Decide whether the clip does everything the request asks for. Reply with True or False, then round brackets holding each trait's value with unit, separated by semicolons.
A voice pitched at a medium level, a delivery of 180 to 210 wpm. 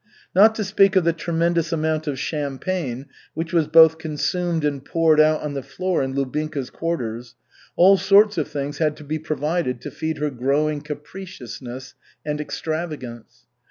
False (155 Hz; 160 wpm)